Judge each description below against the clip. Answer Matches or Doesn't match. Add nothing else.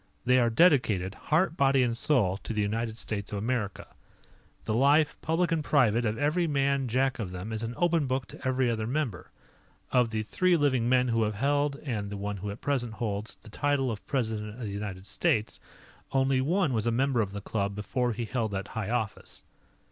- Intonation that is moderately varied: Matches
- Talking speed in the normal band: Doesn't match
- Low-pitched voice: Matches